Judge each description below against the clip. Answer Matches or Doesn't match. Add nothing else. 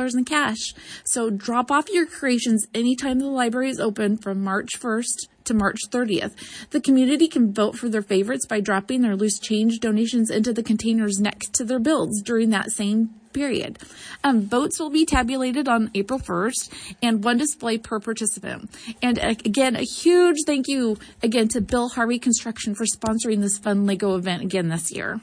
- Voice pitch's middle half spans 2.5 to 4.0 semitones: Matches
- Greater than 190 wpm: Doesn't match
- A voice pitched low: Doesn't match